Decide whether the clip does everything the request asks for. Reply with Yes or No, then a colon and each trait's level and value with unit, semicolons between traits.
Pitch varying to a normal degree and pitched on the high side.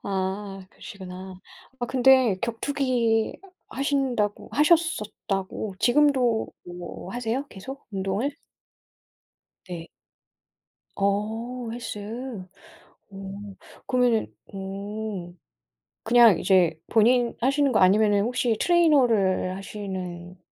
Yes: average, 4.4 semitones; high, 215 Hz